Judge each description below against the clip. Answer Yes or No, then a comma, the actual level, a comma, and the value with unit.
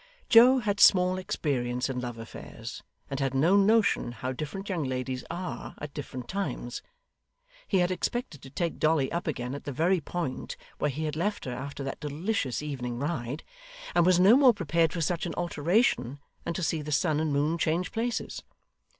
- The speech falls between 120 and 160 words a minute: No, average, 185 wpm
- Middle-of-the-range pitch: Yes, medium, 155 Hz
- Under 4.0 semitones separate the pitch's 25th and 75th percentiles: No, average, 5.2 semitones